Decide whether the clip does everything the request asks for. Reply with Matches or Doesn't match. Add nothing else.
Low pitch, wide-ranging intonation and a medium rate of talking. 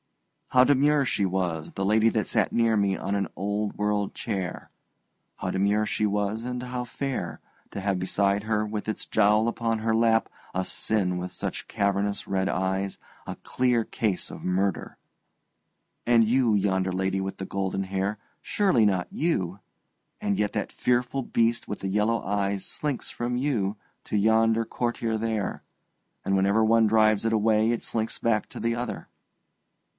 Doesn't match